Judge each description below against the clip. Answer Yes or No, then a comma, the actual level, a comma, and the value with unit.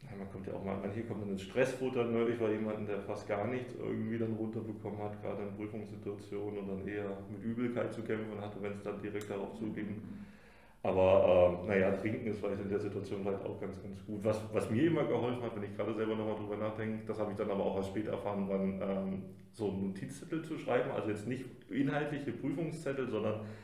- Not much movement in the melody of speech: Yes, narrow, 1.7 semitones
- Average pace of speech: No, fast, 235 wpm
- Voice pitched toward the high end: No, low, 105 Hz